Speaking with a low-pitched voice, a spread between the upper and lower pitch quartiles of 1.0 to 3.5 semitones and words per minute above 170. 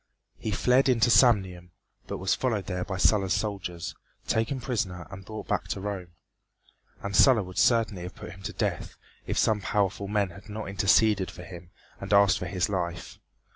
Yes: low, 100 Hz; average, 3.0 semitones; average, 180 wpm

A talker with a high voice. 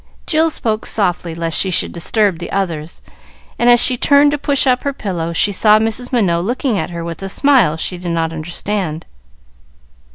Yes: high, 195 Hz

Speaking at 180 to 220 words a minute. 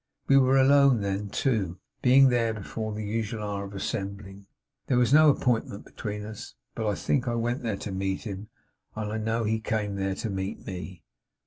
Yes: average, 195 wpm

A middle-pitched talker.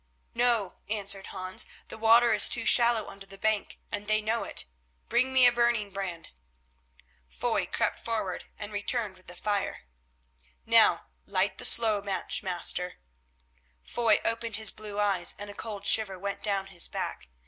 No: high, 205 Hz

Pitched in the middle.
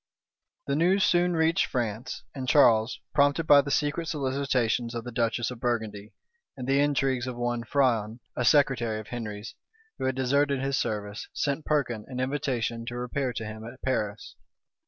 No: low, 125 Hz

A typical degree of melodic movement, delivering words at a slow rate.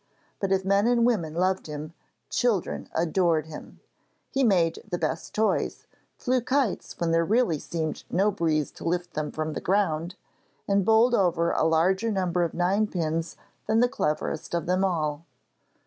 No: average, 4.0 semitones; average, 165 wpm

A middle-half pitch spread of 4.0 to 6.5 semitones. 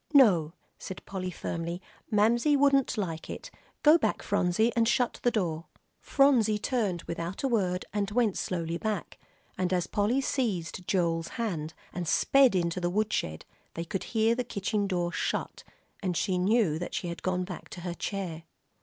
Yes: average, 4.6 semitones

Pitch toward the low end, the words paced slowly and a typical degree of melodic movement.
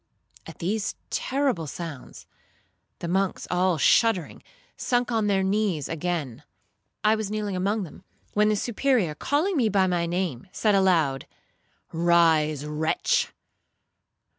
No: medium, 185 Hz; slow, 125 wpm; average, 4.5 semitones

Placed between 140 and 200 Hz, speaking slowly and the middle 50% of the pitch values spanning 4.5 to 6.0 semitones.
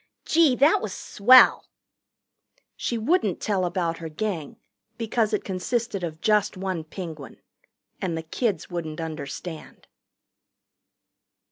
Yes: medium, 185 Hz; slow, 115 wpm; average, 5.1 semitones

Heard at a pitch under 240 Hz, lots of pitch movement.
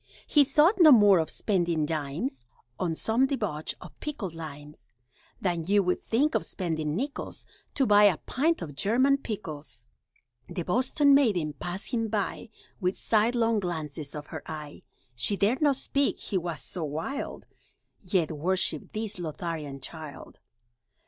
Yes: medium, 185 Hz; wide, 6.8 semitones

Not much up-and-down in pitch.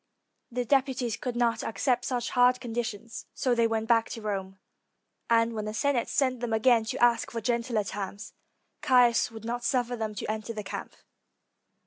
Yes: narrow, 1.9 semitones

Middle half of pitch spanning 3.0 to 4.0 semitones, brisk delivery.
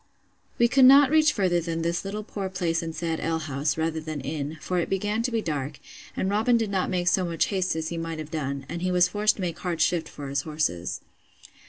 Yes: average, 3.7 semitones; fast, 235 wpm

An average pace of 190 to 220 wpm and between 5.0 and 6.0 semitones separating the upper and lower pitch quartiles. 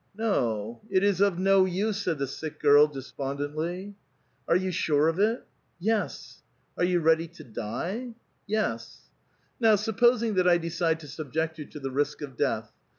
Yes: average, 195 wpm; wide, 5.5 semitones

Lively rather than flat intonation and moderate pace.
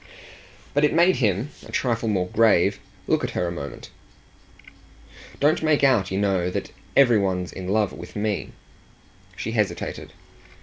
Yes: wide, 5.7 semitones; average, 155 wpm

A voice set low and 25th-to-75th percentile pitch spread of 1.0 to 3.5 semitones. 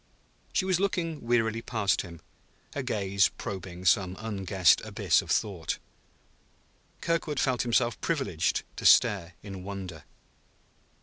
No: low, 100 Hz; average, 4.7 semitones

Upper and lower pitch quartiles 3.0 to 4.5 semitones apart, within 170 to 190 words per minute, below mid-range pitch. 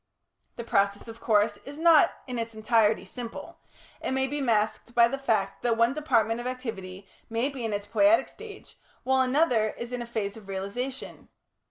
No: average, 3.6 semitones; average, 185 wpm; high, 235 Hz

